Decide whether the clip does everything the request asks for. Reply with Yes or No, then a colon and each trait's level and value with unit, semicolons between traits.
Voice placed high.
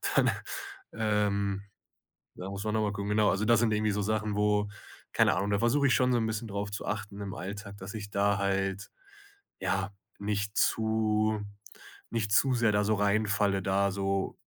No: low, 105 Hz